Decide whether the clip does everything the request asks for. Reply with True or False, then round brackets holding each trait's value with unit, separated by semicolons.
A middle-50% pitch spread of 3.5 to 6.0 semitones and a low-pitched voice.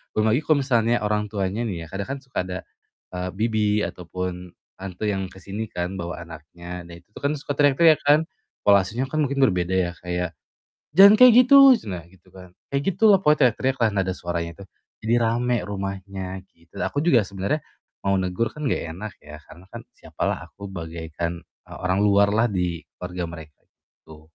True (4.8 semitones; 100 Hz)